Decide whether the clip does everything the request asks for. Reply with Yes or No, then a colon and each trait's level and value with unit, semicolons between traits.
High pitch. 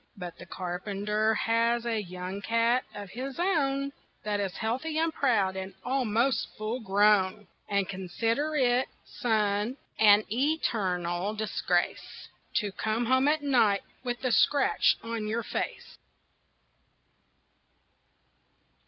Yes: high, 220 Hz